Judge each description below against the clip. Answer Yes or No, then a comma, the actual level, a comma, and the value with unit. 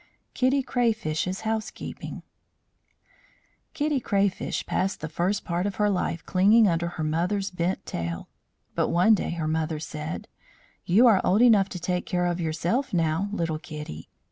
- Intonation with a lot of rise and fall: No, average, 4.2 semitones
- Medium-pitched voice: Yes, medium, 180 Hz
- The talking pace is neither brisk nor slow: Yes, average, 150 wpm